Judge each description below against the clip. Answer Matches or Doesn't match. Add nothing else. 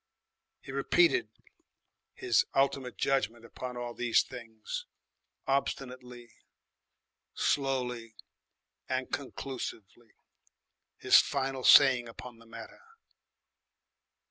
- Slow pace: Matches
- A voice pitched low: Matches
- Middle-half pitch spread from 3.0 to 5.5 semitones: Doesn't match